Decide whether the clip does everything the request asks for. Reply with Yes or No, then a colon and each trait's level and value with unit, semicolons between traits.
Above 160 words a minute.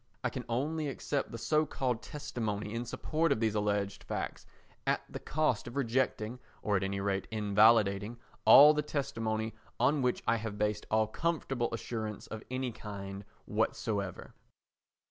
No: average, 155 wpm